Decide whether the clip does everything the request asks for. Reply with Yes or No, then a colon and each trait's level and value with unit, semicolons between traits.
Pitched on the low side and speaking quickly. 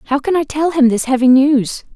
No: very high, 275 Hz; fast, 245 wpm